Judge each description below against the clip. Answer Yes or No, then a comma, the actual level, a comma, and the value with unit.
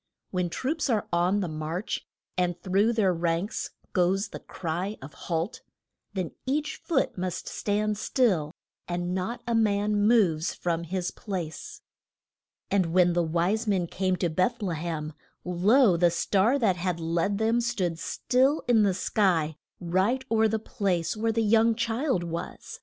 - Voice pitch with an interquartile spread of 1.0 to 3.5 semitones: No, average, 4.2 semitones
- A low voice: No, medium, 185 Hz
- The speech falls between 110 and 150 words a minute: No, average, 160 wpm